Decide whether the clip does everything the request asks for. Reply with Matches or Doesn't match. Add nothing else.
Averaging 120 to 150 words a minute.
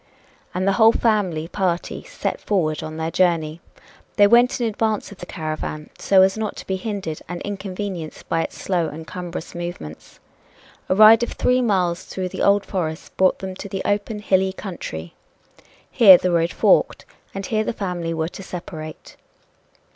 Doesn't match